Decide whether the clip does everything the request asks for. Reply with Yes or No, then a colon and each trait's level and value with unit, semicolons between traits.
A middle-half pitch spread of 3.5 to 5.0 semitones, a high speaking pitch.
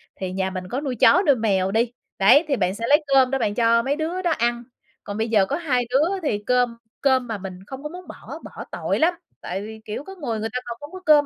No: wide, 5.4 semitones; high, 245 Hz